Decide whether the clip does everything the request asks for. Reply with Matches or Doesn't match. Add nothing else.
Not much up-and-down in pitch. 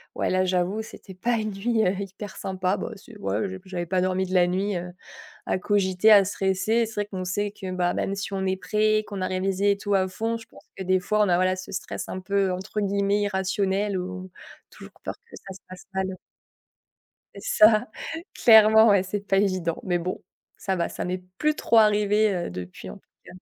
Matches